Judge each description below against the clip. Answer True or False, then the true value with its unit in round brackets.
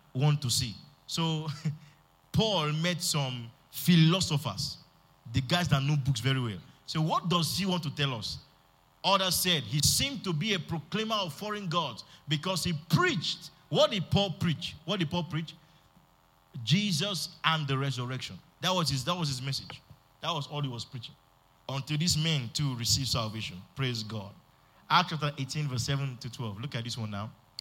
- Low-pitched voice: False (150 Hz)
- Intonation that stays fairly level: False (4.3 semitones)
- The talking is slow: False (180 wpm)